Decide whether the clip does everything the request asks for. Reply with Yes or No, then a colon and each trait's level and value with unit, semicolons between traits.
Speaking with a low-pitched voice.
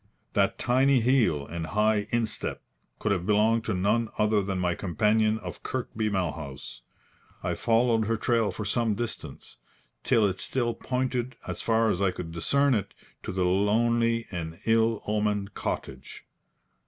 Yes: low, 110 Hz